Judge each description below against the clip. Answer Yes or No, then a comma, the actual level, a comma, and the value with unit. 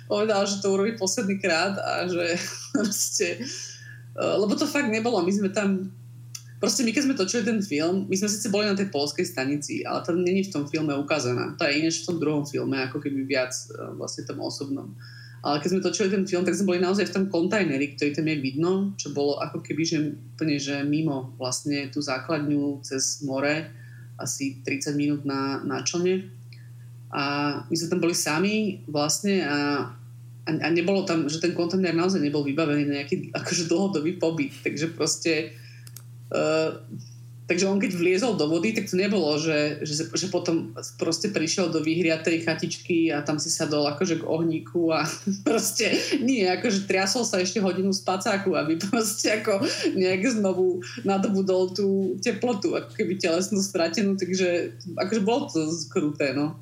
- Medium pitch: Yes, medium, 165 Hz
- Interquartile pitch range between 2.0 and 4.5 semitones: No, average, 4.9 semitones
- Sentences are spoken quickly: Yes, fast, 175 wpm